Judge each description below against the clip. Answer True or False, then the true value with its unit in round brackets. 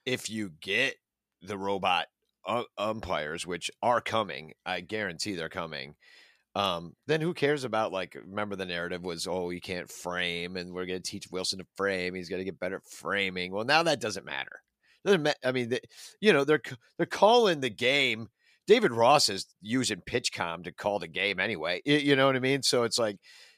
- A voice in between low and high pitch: False (100 Hz)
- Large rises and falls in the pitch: True (6.4 semitones)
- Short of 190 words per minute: False (200 wpm)